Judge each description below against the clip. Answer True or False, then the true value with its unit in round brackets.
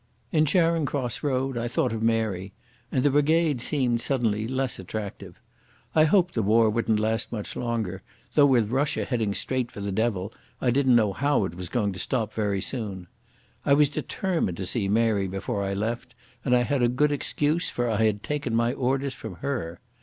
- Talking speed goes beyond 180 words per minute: True (195 wpm)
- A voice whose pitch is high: False (120 Hz)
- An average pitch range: True (4.6 semitones)